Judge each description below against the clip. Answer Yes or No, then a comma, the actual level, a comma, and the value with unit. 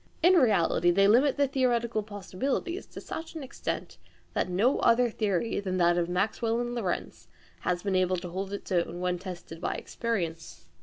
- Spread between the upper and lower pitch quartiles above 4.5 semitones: Yes, average, 5.1 semitones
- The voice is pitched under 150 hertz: No, high, 200 Hz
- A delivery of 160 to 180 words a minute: Yes, average, 175 wpm